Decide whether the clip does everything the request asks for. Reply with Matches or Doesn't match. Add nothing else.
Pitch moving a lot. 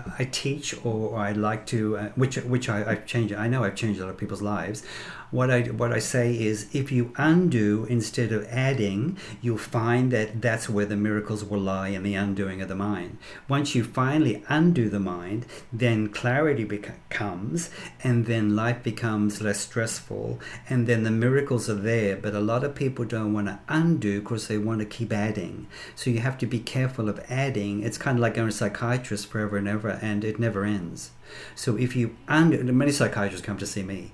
Doesn't match